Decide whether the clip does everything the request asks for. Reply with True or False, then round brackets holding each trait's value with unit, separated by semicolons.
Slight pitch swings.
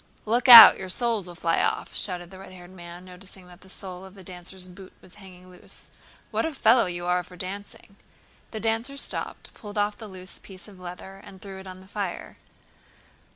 True (2.3 semitones)